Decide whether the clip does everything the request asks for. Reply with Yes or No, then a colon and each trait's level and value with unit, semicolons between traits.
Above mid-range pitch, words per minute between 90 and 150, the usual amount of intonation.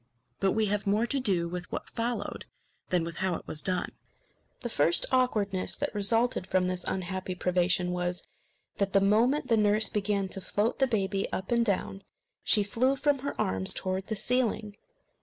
No: high, 200 Hz; average, 180 wpm; average, 3.7 semitones